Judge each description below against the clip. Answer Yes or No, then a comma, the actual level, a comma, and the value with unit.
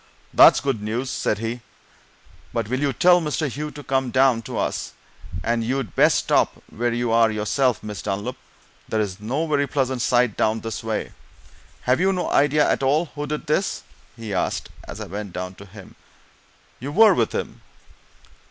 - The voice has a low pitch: Yes, low, 125 Hz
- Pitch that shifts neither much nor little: Yes, average, 4.7 semitones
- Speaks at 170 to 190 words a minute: Yes, average, 180 wpm